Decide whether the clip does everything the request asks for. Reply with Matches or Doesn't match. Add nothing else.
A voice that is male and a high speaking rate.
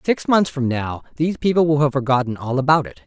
Matches